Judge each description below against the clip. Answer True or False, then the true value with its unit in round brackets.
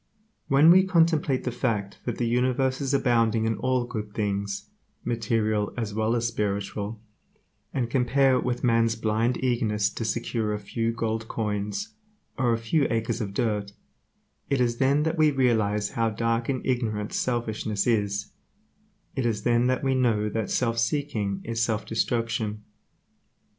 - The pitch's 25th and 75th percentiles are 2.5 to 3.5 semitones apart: True (2.9 semitones)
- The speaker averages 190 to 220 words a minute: False (160 wpm)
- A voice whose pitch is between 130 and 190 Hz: False (115 Hz)